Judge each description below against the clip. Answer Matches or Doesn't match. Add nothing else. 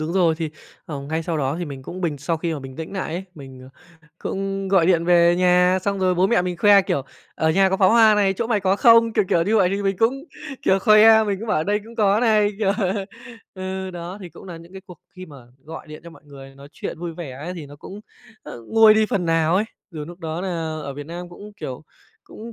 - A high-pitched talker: Doesn't match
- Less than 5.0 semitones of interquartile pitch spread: Matches